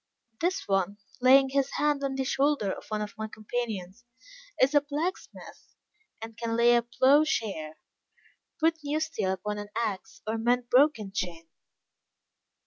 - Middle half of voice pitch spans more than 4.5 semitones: Yes, average, 5.3 semitones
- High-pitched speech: Yes, high, 240 Hz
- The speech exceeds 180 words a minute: No, average, 150 wpm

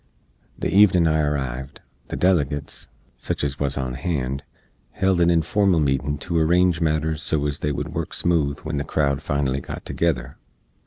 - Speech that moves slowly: No, average, 165 wpm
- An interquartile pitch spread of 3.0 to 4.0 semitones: Yes, average, 3.4 semitones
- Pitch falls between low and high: No, very low, 75 Hz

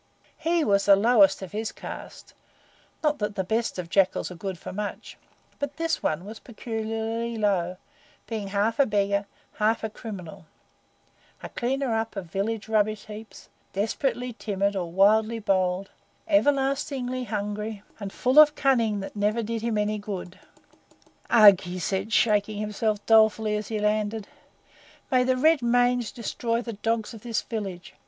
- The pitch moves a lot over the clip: No, narrow, 2.6 semitones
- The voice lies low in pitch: No, high, 215 Hz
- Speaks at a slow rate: No, average, 155 wpm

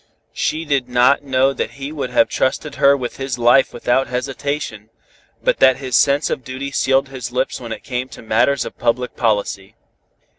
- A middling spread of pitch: No, narrow, 2.2 semitones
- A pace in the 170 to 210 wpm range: Yes, average, 185 wpm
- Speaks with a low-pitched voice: Yes, low, 130 Hz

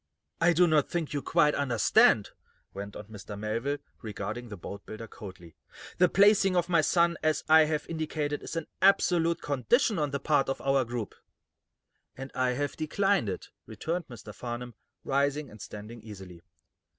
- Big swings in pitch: Yes, wide, 6.7 semitones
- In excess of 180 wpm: No, average, 165 wpm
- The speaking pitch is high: No, medium, 140 Hz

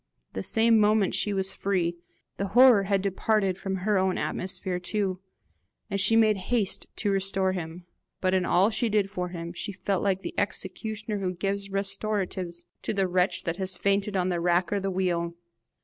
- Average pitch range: No, narrow, 2.0 semitones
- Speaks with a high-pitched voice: Yes, high, 195 Hz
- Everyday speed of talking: Yes, average, 185 wpm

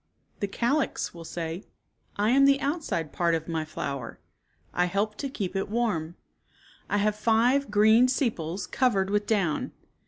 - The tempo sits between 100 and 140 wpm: No, average, 165 wpm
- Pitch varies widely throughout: Yes, wide, 5.8 semitones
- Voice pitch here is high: Yes, high, 205 Hz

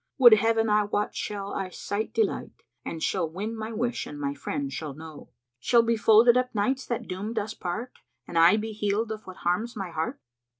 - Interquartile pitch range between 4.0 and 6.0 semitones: Yes, average, 4.3 semitones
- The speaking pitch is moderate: No, high, 210 Hz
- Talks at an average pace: No, fast, 215 wpm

